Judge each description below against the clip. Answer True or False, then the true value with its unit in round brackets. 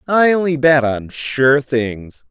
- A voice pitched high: False (140 Hz)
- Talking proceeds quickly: False (155 wpm)